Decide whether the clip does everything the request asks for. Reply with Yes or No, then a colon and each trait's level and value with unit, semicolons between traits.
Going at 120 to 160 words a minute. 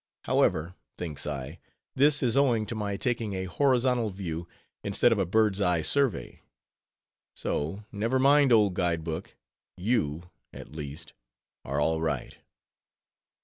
Yes: slow, 135 wpm